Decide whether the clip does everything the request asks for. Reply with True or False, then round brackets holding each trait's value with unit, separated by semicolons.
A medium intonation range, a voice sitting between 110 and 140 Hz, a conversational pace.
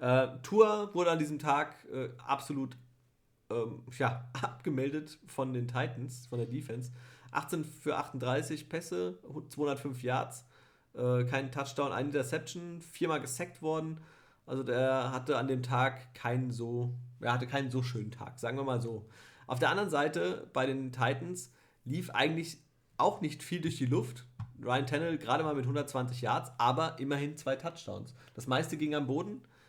True (3.3 semitones; 135 Hz; 160 wpm)